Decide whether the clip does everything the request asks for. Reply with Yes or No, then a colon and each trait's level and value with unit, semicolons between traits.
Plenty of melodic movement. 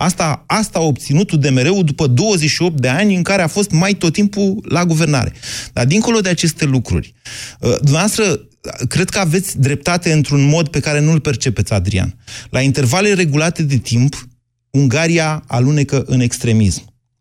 Yes: wide, 5.7 semitones